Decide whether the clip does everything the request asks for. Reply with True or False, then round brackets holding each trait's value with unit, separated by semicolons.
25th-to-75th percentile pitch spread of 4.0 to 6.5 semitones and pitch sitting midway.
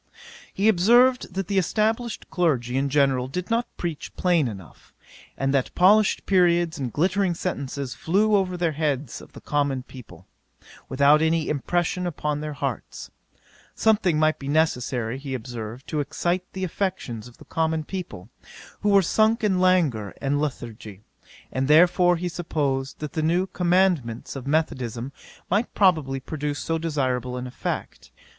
True (5.4 semitones; 155 Hz)